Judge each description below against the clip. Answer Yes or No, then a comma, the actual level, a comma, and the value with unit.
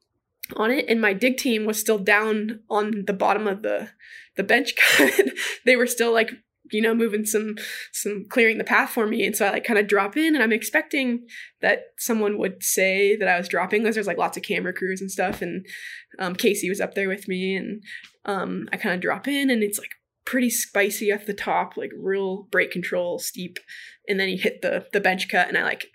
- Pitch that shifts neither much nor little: Yes, average, 3.0 semitones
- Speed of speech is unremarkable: No, fast, 225 wpm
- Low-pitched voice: No, high, 210 Hz